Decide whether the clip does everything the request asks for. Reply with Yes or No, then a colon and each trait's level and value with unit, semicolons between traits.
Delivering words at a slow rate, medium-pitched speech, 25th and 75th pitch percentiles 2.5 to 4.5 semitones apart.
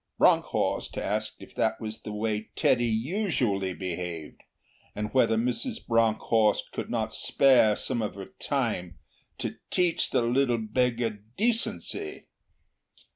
No: slow, 125 wpm; low, 115 Hz; average, 3.6 semitones